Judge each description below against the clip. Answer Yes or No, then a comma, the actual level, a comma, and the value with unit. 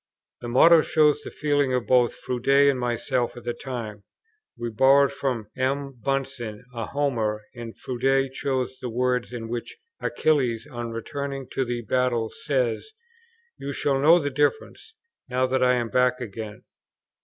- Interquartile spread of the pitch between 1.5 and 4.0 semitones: Yes, narrow, 2.6 semitones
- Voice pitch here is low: Yes, low, 125 Hz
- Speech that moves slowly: No, average, 155 wpm